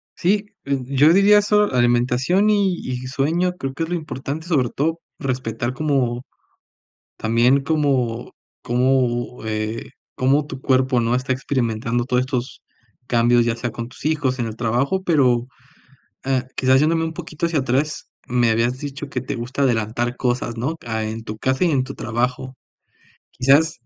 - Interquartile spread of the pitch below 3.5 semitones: No, average, 3.8 semitones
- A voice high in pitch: No, low, 130 Hz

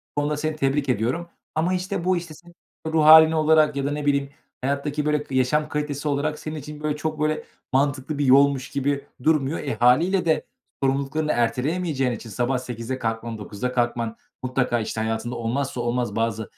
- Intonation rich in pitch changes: No, average, 3.6 semitones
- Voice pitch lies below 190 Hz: Yes, medium, 140 Hz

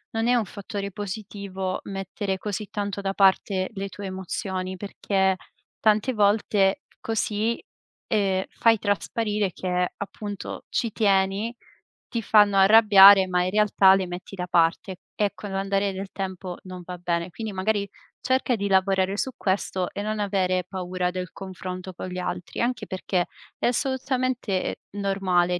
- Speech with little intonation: Yes, narrow, 2.0 semitones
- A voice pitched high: Yes, high, 195 Hz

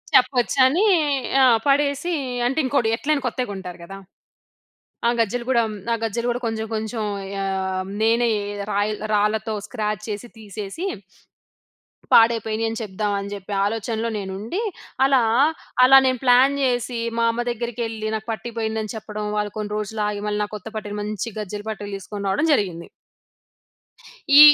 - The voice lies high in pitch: Yes, high, 220 Hz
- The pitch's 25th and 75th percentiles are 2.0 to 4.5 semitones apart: Yes, average, 2.8 semitones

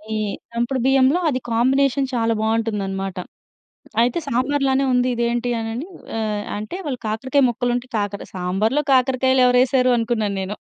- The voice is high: Yes, high, 240 Hz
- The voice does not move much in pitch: No, average, 3.1 semitones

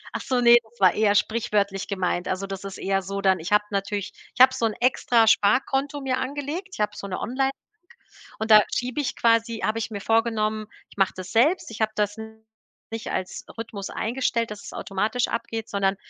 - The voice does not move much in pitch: No, average, 3.2 semitones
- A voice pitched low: No, high, 220 Hz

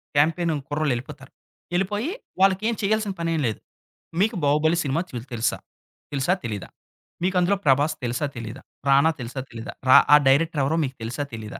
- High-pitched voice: No, medium, 145 Hz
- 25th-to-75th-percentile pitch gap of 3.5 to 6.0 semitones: Yes, average, 5.3 semitones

